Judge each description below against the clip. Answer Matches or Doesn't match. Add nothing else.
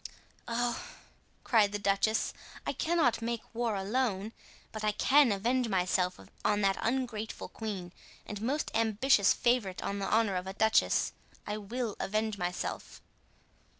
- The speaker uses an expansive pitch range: Doesn't match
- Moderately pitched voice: Doesn't match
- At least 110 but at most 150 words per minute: Matches